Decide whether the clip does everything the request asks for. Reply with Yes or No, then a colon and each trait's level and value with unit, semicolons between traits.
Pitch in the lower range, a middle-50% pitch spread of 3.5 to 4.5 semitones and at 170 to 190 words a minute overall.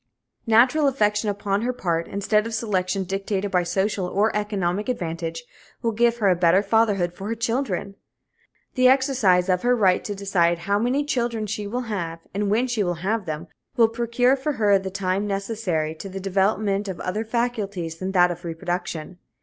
No: high, 200 Hz; average, 3.8 semitones; average, 180 wpm